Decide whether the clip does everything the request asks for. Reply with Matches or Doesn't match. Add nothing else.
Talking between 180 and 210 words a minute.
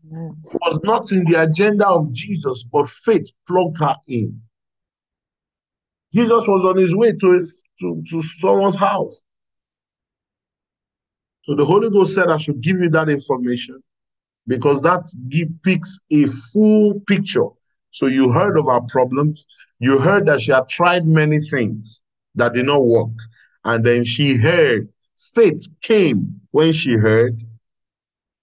Doesn't match